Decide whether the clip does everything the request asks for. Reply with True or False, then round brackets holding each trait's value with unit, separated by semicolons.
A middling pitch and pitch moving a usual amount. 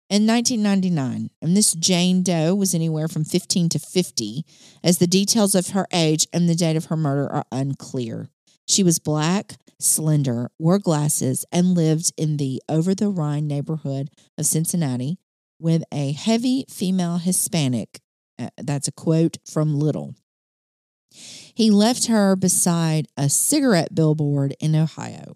True (165 Hz; 3.7 semitones)